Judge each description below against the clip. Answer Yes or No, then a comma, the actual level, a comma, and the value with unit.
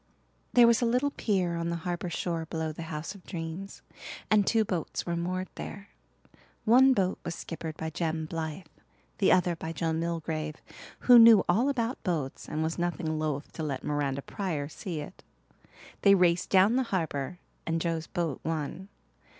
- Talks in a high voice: No, medium, 170 Hz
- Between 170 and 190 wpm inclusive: Yes, average, 175 wpm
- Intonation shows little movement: No, average, 3.5 semitones